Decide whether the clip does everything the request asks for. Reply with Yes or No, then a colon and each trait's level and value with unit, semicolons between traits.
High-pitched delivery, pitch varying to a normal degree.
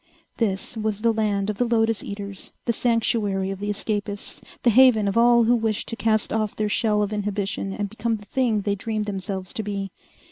No: high, 210 Hz; narrow, 2.1 semitones